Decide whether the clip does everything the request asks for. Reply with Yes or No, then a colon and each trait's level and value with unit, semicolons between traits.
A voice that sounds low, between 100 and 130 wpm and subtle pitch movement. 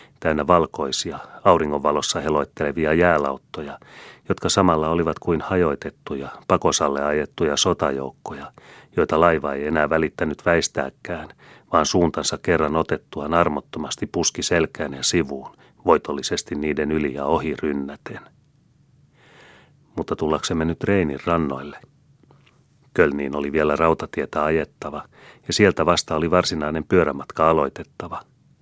Yes: very low, 75 Hz; average, 105 wpm; narrow, 2.2 semitones